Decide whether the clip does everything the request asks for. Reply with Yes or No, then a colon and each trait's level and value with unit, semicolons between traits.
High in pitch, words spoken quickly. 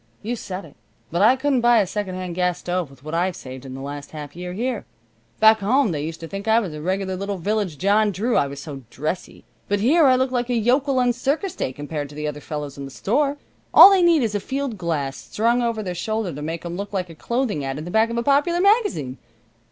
Yes: high, 195 Hz; fast, 255 wpm